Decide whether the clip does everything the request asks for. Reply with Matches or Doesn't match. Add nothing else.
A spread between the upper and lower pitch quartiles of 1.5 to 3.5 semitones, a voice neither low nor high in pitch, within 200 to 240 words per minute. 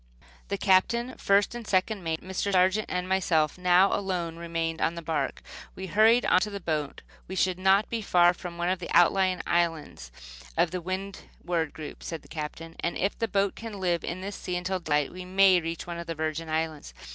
Matches